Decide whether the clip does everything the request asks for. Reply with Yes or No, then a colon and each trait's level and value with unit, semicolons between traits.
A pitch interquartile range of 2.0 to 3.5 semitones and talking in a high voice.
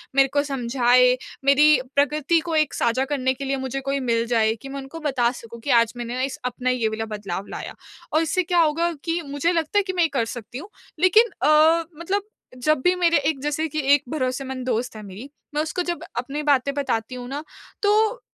No: average, 4.2 semitones; very high, 275 Hz